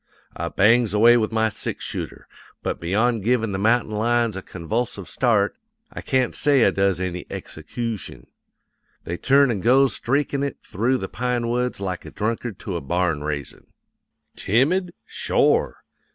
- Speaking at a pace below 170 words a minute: Yes, average, 155 wpm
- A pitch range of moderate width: Yes, average, 4.2 semitones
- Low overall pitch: Yes, low, 115 Hz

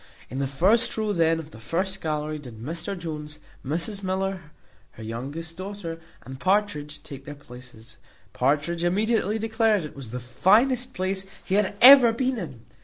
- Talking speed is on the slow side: No, average, 165 wpm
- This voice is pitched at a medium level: Yes, medium, 170 Hz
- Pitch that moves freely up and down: Yes, wide, 6.1 semitones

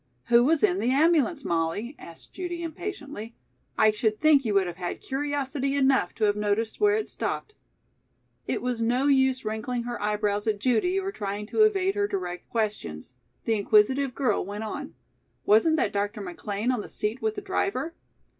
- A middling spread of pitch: No, wide, 6.2 semitones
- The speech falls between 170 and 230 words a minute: Yes, average, 180 wpm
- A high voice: Yes, high, 240 Hz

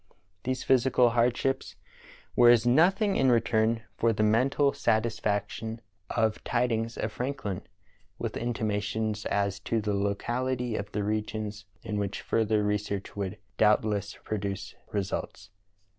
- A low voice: Yes, low, 110 Hz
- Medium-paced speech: No, slow, 130 wpm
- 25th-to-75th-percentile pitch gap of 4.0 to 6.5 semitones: No, average, 2.7 semitones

